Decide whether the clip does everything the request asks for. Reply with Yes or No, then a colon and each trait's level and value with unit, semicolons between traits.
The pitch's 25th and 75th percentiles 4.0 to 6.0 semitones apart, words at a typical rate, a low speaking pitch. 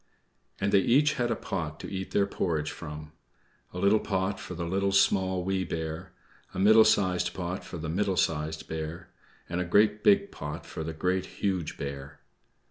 No: average, 3.6 semitones; average, 185 wpm; very low, 90 Hz